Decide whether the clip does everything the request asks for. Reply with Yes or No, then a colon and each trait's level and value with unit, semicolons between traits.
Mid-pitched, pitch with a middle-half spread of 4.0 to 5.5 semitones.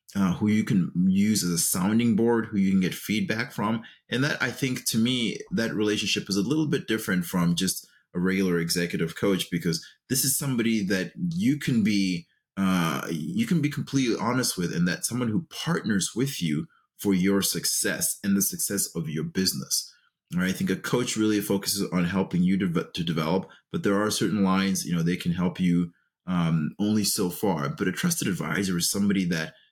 No: low, 100 Hz; average, 4.8 semitones